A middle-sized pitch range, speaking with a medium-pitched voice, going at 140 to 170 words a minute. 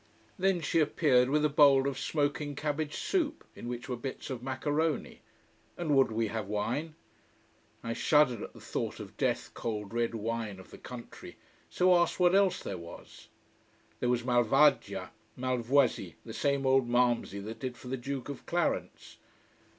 No: average, 4.1 semitones; low, 130 Hz; average, 165 wpm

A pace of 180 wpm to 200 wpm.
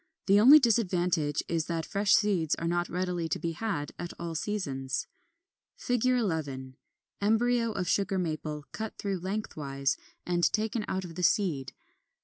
No: average, 155 wpm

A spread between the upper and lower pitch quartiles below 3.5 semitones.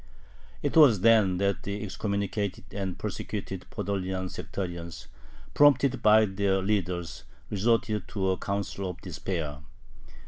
Yes: narrow, 2.4 semitones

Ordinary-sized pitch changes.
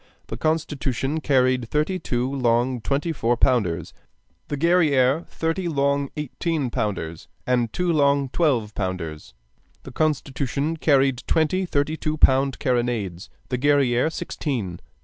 Yes: average, 4.1 semitones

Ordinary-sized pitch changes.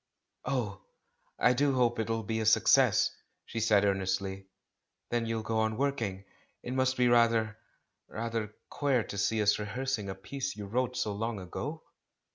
Yes: average, 3.3 semitones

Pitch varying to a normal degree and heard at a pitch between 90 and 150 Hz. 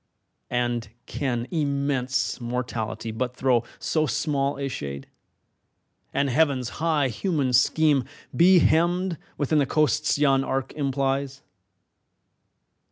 Yes: average, 3.3 semitones; low, 135 Hz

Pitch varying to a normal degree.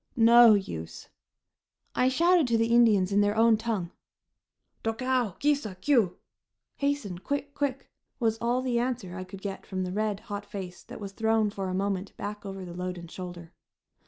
Yes: average, 4.2 semitones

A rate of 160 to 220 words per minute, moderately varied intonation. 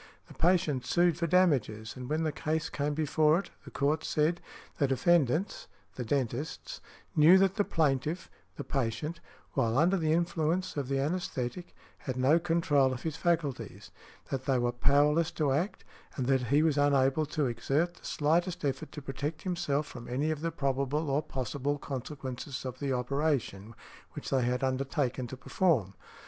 Yes: average, 170 wpm; average, 3.7 semitones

